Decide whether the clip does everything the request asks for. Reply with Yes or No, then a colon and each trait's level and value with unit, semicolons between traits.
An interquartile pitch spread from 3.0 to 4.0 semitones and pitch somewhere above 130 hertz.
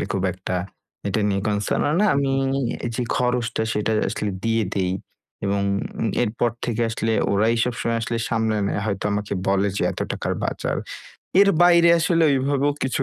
No: average, 3.7 semitones; low, 115 Hz